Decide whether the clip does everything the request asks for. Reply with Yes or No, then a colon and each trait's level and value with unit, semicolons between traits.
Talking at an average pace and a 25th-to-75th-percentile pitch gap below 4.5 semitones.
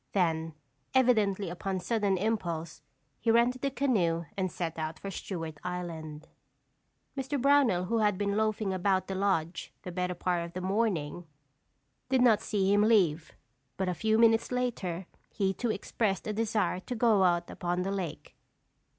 Yes: average, 160 wpm; average, 4.1 semitones